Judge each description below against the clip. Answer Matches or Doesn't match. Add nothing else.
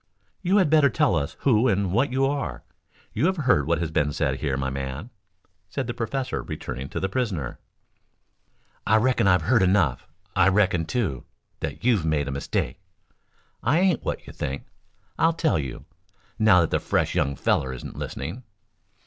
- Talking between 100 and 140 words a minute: Doesn't match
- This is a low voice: Matches